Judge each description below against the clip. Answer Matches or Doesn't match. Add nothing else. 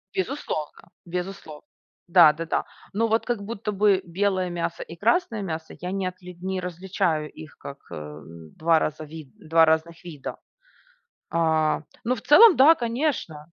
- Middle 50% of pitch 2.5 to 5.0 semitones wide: Matches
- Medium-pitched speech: Matches